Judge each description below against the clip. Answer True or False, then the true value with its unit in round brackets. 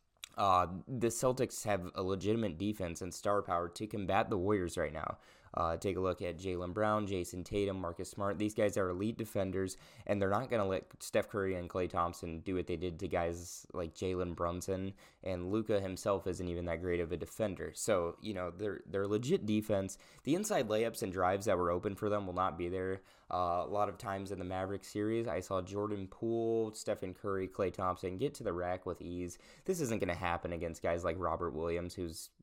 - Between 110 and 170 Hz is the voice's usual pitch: False (95 Hz)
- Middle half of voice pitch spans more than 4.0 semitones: False (2.7 semitones)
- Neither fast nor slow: False (215 wpm)